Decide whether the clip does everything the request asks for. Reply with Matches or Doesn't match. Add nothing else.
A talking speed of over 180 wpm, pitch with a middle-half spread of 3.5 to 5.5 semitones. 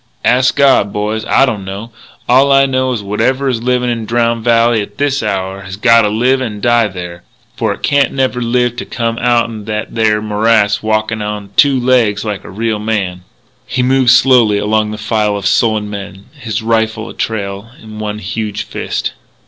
Doesn't match